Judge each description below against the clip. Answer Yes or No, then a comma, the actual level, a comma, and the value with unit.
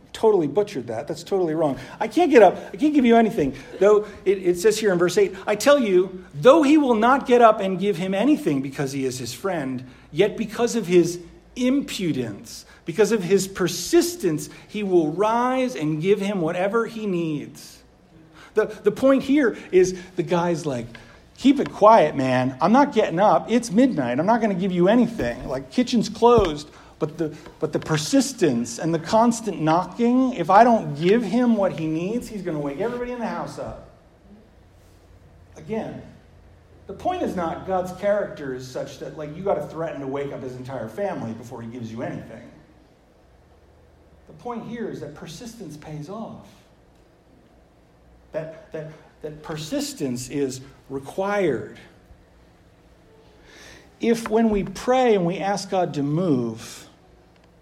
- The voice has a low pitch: No, medium, 180 Hz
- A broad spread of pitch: Yes, wide, 7.3 semitones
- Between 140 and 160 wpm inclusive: No, average, 170 wpm